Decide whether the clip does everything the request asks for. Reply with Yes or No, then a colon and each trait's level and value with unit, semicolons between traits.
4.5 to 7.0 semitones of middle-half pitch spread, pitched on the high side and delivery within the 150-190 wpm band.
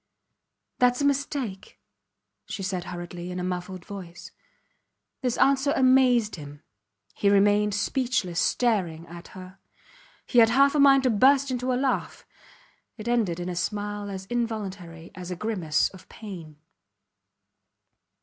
No: wide, 5.6 semitones; high, 205 Hz; average, 140 wpm